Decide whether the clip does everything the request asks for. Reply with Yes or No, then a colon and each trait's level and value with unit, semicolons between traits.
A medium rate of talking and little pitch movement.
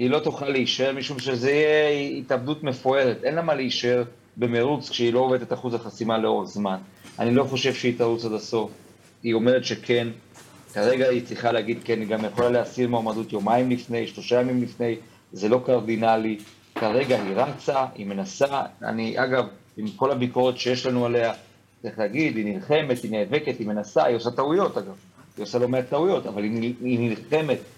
No: fast, 180 wpm; narrow, 2.3 semitones